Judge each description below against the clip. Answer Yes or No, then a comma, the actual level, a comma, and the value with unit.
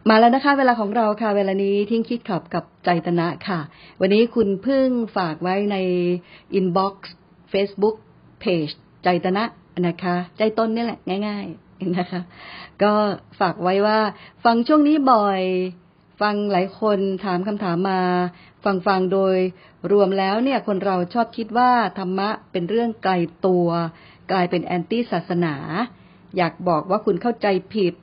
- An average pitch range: Yes, average, 3.1 semitones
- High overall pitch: Yes, high, 195 Hz